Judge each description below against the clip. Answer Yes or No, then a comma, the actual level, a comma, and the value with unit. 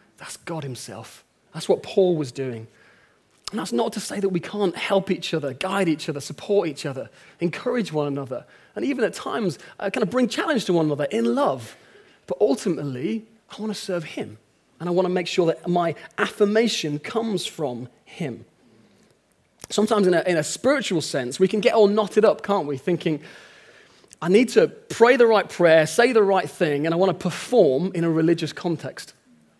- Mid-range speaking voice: Yes, medium, 180 Hz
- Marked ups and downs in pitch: Yes, wide, 5.7 semitones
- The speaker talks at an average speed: Yes, average, 195 wpm